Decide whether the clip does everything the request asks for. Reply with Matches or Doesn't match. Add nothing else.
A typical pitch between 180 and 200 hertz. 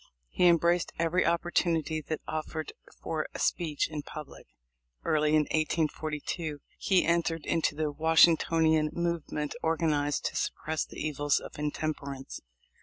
Doesn't match